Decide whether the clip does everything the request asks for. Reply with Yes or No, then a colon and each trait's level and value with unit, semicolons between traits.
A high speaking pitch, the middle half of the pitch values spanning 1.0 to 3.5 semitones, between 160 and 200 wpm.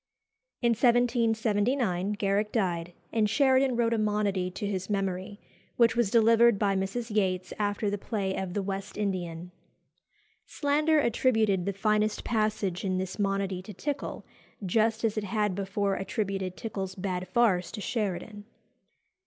No: high, 205 Hz; average, 2.9 semitones; average, 145 wpm